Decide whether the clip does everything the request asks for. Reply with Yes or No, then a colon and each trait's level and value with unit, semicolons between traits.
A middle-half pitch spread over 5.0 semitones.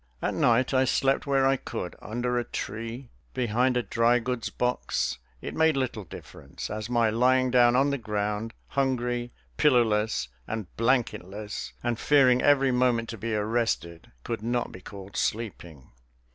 No: average, 2.9 semitones